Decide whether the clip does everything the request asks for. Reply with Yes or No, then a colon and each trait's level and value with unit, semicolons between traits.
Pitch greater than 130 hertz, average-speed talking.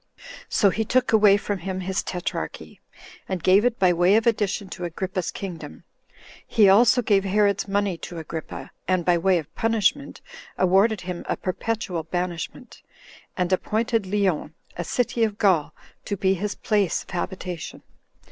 Yes: high, 190 Hz; average, 155 wpm